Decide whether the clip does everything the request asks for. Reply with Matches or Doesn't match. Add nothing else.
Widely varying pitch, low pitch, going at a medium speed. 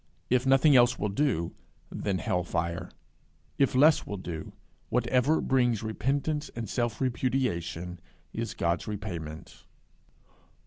Doesn't match